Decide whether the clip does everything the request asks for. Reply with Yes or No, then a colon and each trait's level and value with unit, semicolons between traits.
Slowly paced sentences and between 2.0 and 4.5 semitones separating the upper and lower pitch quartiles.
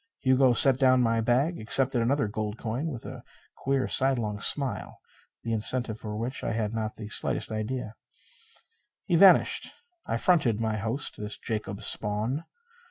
No: average, 160 wpm; average, 3.6 semitones